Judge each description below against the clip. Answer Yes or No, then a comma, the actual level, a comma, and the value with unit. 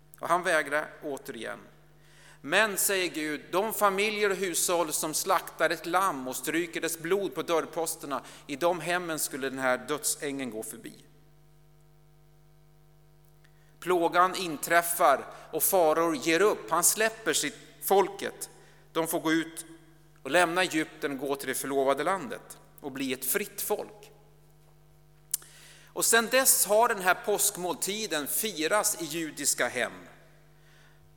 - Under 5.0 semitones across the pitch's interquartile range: Yes, average, 2.9 semitones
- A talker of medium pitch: Yes, medium, 160 Hz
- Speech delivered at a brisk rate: No, average, 130 wpm